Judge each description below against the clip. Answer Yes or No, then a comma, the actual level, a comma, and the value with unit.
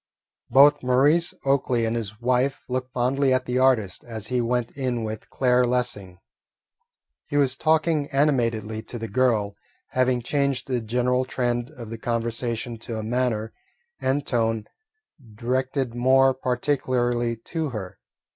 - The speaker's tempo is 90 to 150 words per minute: Yes, average, 140 wpm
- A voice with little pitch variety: Yes, narrow, 2.2 semitones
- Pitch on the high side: No, low, 125 Hz